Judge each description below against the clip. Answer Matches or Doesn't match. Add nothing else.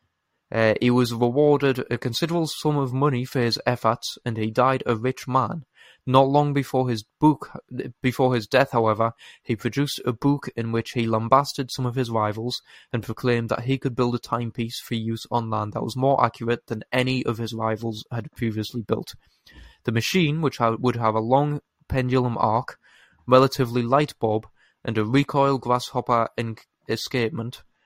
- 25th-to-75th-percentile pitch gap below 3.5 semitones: Matches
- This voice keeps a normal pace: Matches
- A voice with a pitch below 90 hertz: Doesn't match